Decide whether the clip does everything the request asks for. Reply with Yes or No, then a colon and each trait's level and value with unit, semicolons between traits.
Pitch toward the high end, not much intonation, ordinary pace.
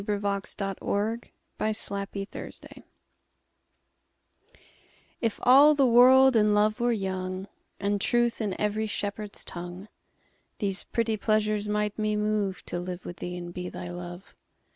No: high, 210 Hz; narrow, 2.3 semitones; slow, 130 wpm